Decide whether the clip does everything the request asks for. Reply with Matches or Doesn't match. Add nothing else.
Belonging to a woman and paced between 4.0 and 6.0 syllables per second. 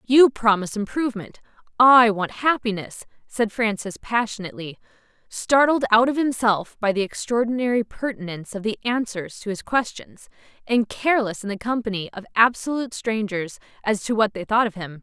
Matches